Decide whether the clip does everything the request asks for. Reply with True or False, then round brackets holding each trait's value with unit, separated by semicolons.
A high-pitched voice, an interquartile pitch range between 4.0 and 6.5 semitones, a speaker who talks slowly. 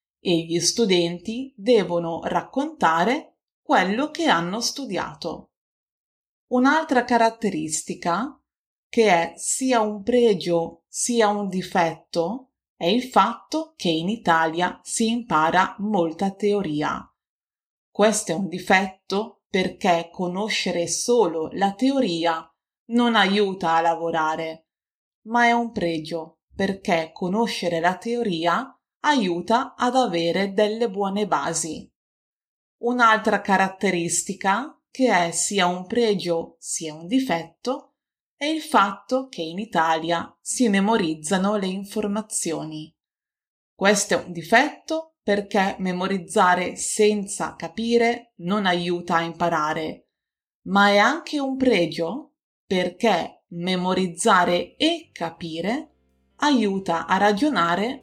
True (195 Hz; 5.4 semitones; 105 wpm)